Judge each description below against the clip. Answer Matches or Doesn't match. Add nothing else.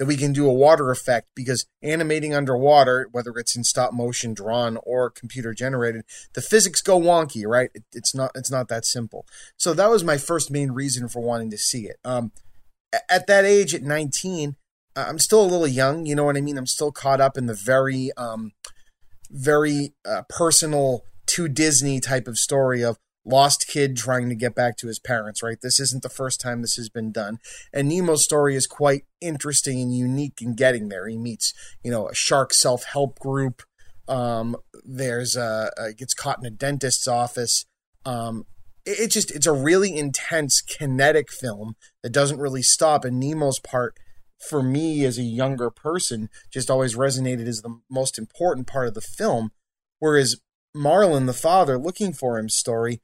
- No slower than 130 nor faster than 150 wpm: Doesn't match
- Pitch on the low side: Matches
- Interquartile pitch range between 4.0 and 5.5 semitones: Doesn't match